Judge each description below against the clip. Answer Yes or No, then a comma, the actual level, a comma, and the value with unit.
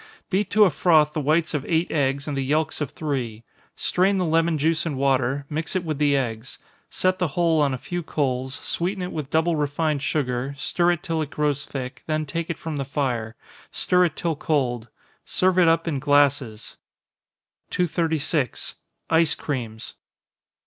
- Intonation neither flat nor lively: Yes, average, 3.4 semitones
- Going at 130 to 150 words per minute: No, average, 180 wpm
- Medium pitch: Yes, medium, 150 Hz